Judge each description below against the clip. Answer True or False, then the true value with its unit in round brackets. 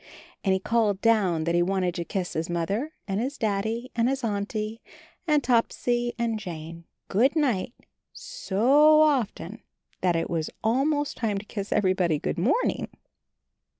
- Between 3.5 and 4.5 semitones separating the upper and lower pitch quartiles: False (4.9 semitones)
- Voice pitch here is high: True (215 Hz)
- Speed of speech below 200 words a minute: True (150 wpm)